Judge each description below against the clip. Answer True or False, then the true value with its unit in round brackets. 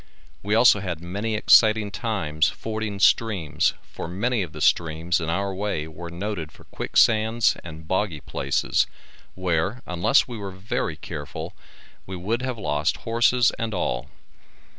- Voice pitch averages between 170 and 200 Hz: False (95 Hz)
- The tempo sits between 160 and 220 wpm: False (145 wpm)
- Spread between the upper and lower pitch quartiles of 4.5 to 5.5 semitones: True (5.1 semitones)